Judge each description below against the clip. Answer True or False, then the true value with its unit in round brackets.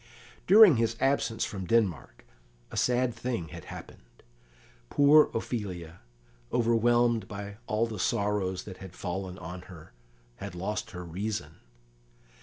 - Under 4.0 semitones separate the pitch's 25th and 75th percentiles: False (4.4 semitones)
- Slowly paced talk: True (125 wpm)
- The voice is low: True (105 Hz)